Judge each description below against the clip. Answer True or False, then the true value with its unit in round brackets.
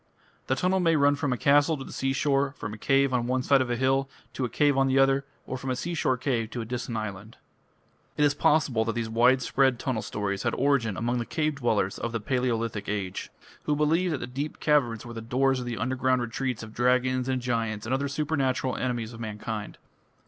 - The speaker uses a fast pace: True (220 wpm)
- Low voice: True (130 Hz)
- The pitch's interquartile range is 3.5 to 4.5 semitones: False (3.1 semitones)